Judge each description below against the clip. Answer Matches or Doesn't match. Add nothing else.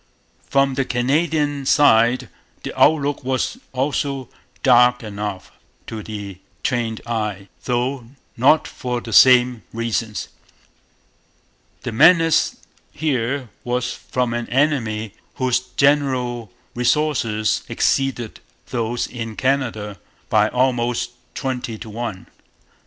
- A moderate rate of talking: Doesn't match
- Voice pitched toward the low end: Matches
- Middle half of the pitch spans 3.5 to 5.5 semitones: Doesn't match